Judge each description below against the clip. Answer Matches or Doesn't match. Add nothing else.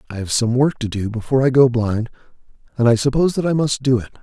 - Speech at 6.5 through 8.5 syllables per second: Matches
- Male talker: Matches